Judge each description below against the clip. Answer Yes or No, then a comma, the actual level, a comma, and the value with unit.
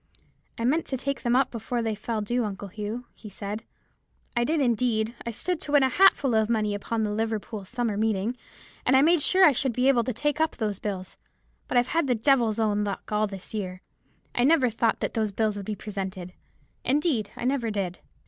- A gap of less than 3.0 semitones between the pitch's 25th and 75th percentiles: No, average, 3.6 semitones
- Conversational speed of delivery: No, fast, 215 wpm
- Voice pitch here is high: Yes, high, 225 Hz